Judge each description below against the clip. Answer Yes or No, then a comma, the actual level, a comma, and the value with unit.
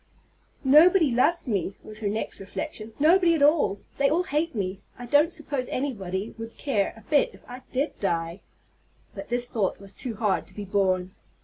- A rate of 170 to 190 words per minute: Yes, average, 185 wpm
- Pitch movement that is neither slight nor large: No, wide, 6.8 semitones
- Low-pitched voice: No, high, 240 Hz